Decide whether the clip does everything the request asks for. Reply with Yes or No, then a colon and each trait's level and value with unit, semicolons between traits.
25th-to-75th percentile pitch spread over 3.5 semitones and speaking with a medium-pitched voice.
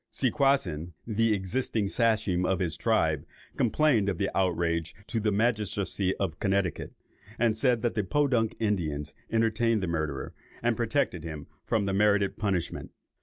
No: average, 4.1 semitones; low, 105 Hz